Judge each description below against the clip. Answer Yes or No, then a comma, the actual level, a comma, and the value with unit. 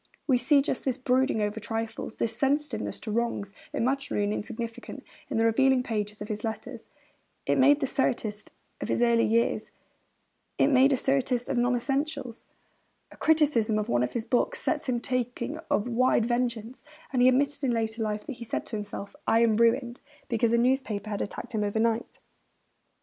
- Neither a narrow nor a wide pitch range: Yes, average, 3.0 semitones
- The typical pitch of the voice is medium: No, high, 235 Hz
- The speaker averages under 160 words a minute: No, average, 185 wpm